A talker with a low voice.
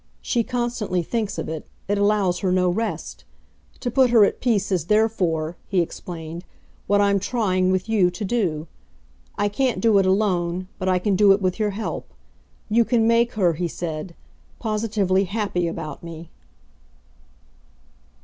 No: high, 195 Hz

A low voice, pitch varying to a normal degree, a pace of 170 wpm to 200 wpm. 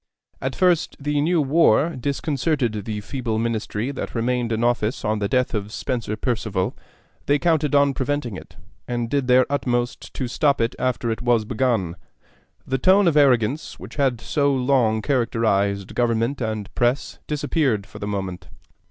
No: low, 125 Hz; average, 4.3 semitones; average, 160 wpm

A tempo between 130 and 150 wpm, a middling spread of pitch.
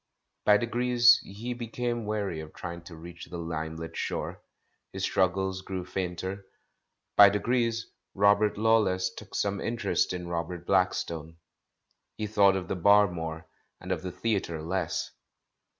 Yes: average, 145 wpm; average, 3.6 semitones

